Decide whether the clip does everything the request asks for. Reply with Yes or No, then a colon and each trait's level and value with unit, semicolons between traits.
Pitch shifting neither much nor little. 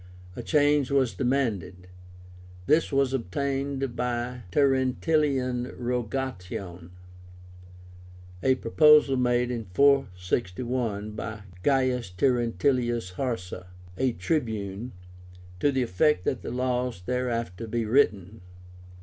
Yes: average, 4.0 semitones